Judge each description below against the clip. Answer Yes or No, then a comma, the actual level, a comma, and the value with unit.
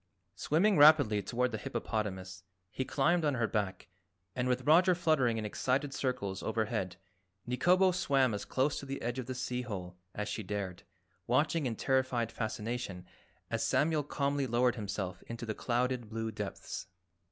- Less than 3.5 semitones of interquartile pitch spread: No, average, 4.7 semitones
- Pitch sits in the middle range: No, low, 125 Hz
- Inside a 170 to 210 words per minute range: No, average, 160 wpm